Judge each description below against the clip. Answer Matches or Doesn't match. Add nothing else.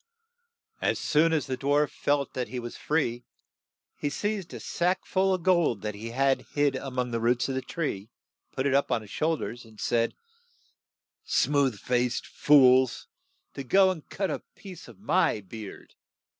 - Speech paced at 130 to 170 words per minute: Doesn't match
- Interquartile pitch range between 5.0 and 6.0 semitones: Doesn't match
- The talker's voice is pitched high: Doesn't match